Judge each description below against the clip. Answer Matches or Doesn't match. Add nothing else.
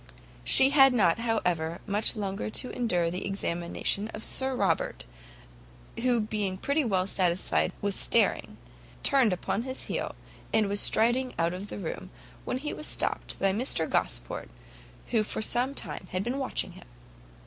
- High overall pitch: Matches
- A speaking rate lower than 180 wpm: Matches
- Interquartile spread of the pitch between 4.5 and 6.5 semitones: Matches